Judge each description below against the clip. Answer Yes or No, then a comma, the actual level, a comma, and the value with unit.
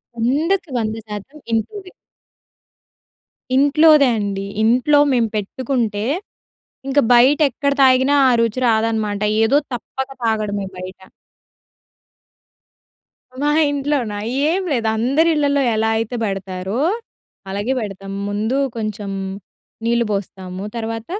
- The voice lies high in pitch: Yes, high, 230 Hz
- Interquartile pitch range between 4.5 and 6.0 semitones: Yes, average, 4.9 semitones